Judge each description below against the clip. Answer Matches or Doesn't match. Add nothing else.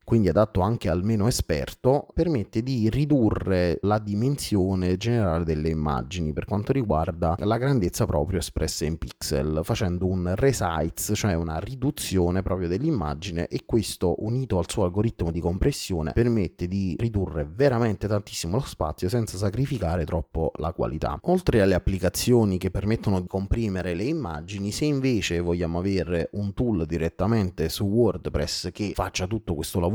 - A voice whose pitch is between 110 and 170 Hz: Doesn't match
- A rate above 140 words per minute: Matches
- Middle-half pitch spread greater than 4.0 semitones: Matches